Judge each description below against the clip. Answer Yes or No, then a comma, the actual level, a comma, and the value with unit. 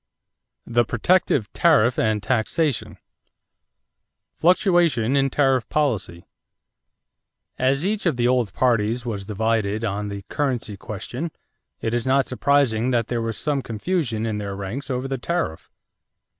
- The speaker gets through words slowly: Yes, slow, 130 wpm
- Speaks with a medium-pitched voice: No, low, 120 Hz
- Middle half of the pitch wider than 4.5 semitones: No, average, 4.2 semitones